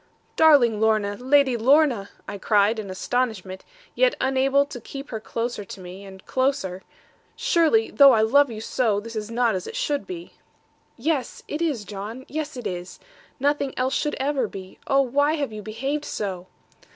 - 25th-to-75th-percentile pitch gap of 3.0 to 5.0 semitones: No, wide, 5.4 semitones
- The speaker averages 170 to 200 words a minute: Yes, average, 175 wpm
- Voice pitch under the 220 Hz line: No, high, 245 Hz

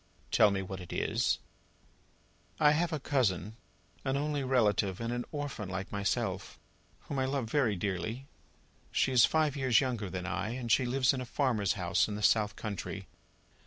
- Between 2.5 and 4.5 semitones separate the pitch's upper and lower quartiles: No, average, 5.1 semitones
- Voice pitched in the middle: No, low, 115 Hz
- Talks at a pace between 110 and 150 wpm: No, average, 175 wpm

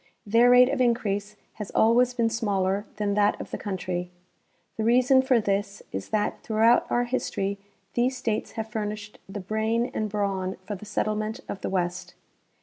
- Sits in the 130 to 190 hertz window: No, high, 215 Hz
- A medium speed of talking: Yes, average, 170 wpm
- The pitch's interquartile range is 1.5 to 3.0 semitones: Yes, average, 2.7 semitones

